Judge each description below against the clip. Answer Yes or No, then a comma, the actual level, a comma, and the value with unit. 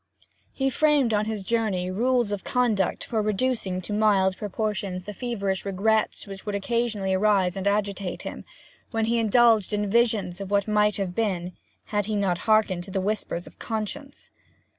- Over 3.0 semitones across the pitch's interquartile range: No, narrow, 2.6 semitones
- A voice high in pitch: Yes, high, 210 Hz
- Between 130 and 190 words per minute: Yes, average, 170 wpm